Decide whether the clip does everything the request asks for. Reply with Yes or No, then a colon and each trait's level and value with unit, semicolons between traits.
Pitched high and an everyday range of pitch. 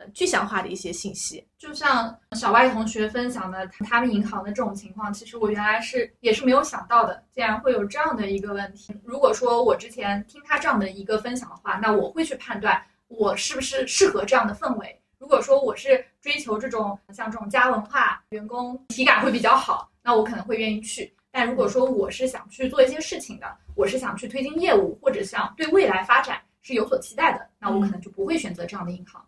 Yes: high, 235 Hz; average, 4.4 semitones